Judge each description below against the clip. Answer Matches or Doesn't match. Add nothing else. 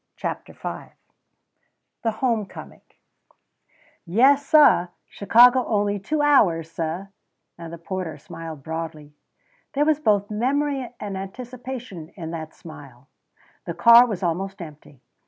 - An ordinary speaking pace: Doesn't match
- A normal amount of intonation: Doesn't match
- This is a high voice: Matches